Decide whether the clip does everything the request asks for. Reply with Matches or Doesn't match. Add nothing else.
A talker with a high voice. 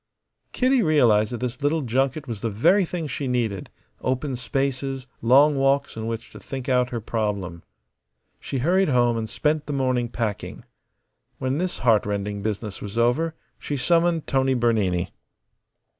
Doesn't match